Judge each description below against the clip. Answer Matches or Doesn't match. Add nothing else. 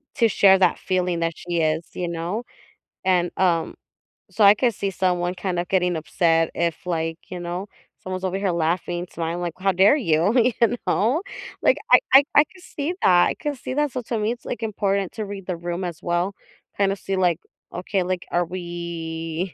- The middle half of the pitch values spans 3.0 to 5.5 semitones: Doesn't match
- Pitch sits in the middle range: Matches